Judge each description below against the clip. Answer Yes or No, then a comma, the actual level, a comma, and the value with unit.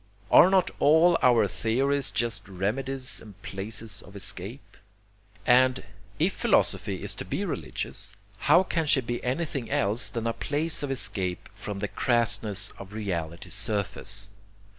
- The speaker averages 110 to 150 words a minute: Yes, average, 140 wpm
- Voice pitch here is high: No, low, 115 Hz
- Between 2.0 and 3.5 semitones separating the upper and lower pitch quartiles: No, average, 5.1 semitones